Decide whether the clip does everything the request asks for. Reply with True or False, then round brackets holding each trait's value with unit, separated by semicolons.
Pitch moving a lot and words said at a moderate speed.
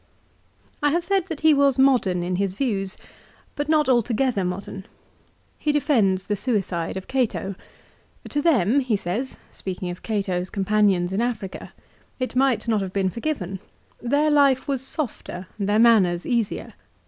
True (6.1 semitones; 165 wpm)